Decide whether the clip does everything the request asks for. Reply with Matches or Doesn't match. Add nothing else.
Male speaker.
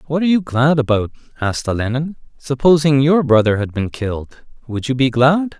Matches